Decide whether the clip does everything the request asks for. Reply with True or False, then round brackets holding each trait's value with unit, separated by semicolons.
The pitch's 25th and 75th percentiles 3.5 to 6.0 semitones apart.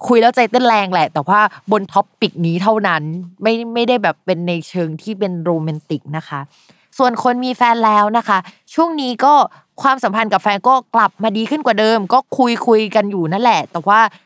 True (4.7 semitones)